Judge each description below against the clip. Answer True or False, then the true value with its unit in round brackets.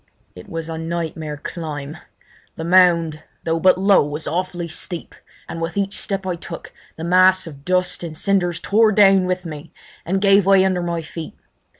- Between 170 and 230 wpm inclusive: True (180 wpm)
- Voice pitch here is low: False (175 Hz)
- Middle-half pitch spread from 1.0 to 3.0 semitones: True (2.5 semitones)